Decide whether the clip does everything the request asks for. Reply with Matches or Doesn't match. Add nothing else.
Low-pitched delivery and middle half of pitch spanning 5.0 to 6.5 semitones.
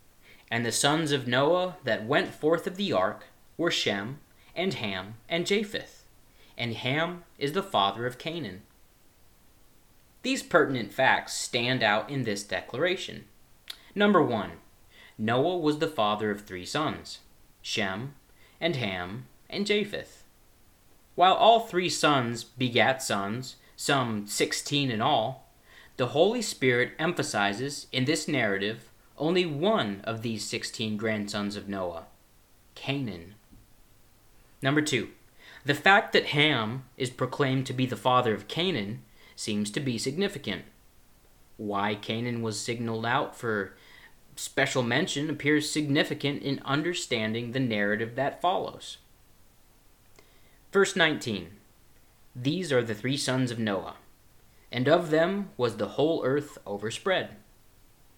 Matches